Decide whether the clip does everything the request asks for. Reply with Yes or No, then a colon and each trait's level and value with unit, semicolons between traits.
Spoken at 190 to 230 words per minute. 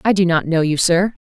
No: fast, 285 wpm